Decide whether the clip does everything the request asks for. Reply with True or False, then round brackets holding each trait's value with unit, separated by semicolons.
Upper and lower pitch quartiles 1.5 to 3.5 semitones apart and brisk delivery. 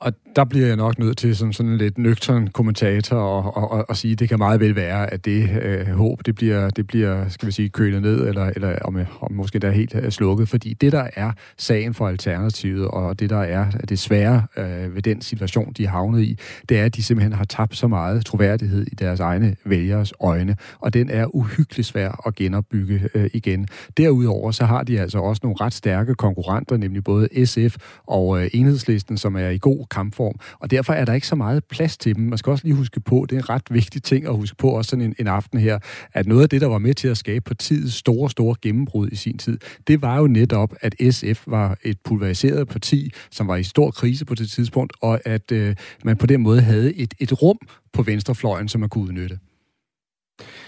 True (3.2 semitones; 235 wpm)